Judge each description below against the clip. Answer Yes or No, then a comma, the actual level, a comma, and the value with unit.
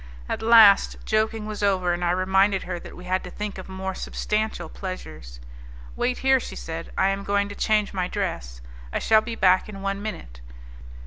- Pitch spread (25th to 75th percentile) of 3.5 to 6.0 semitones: No, average, 2.7 semitones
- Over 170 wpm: Yes, average, 195 wpm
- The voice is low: No, high, 195 Hz